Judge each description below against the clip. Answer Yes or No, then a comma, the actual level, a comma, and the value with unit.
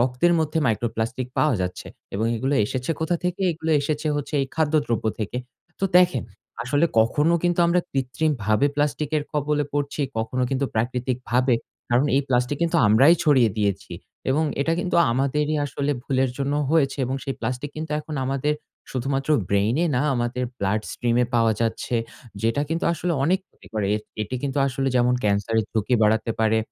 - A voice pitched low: Yes, low, 130 Hz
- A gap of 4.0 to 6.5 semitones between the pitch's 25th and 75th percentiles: Yes, average, 4.3 semitones